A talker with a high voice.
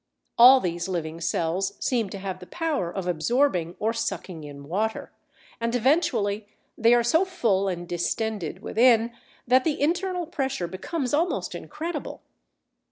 Yes: high, 220 Hz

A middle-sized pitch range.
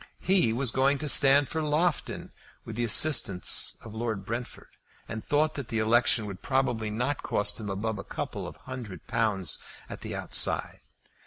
Yes: average, 4.3 semitones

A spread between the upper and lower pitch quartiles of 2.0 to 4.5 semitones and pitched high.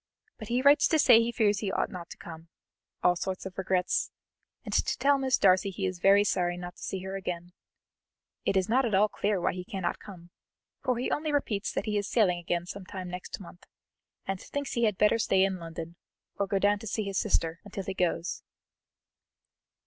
Yes: average, 3.0 semitones; high, 195 Hz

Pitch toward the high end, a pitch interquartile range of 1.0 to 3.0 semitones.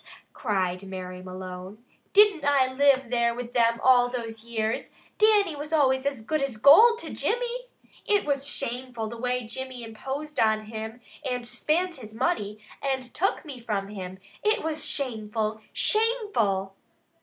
No: very high, 250 Hz; average, 5.0 semitones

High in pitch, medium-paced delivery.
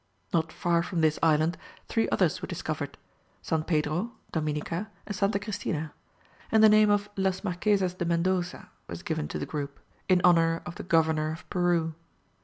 No: medium, 170 Hz; average, 170 wpm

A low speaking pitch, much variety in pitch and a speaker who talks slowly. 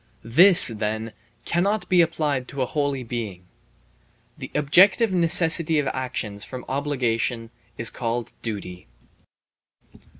Yes: low, 130 Hz; wide, 6.2 semitones; slow, 110 wpm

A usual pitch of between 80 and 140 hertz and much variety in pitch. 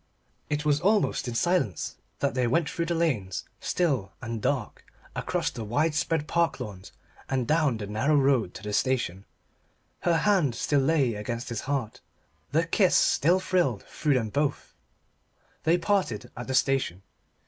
Yes: low, 135 Hz; wide, 6.1 semitones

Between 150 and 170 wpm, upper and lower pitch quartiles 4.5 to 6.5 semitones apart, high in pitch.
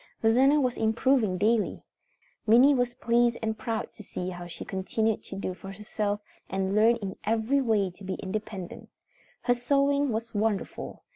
No: average, 160 wpm; average, 3.5 semitones; high, 220 Hz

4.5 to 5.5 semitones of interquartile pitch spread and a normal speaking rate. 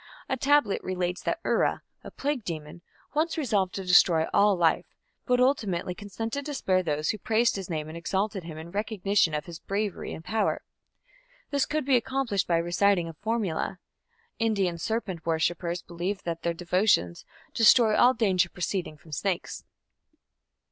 Yes: average, 4.8 semitones; average, 160 wpm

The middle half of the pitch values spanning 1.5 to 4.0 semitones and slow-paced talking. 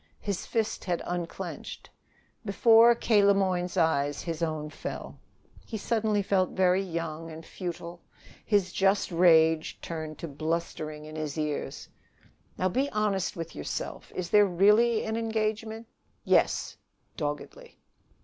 No: average, 4.5 semitones; slow, 130 wpm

